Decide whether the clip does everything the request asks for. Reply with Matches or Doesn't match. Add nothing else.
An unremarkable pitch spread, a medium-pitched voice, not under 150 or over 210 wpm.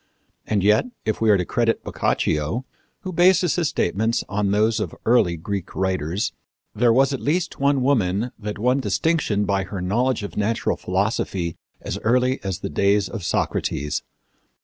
Doesn't match